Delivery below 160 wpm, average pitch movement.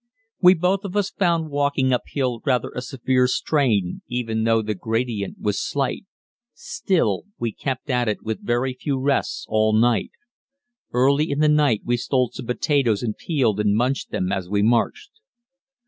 No: average, 165 wpm; average, 4.3 semitones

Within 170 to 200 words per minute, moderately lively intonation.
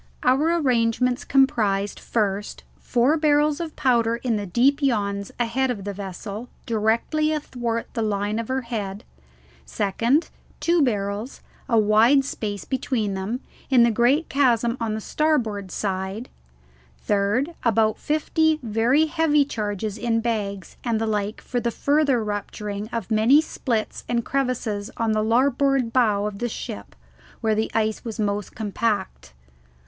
No: average, 145 wpm; average, 4.0 semitones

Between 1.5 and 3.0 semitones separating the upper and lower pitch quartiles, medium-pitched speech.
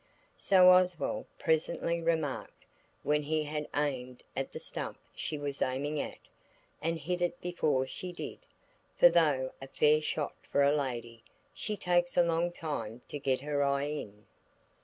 No: average, 3.5 semitones; medium, 150 Hz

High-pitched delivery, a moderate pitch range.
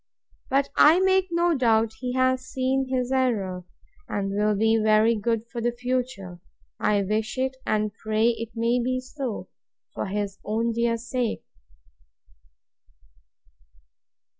Yes: high, 235 Hz; average, 3.2 semitones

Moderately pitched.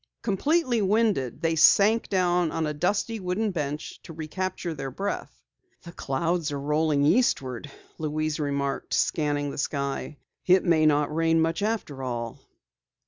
Yes: medium, 160 Hz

